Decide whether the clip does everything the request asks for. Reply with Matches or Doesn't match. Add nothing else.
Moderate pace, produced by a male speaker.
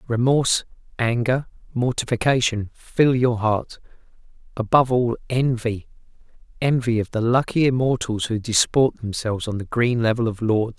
Doesn't match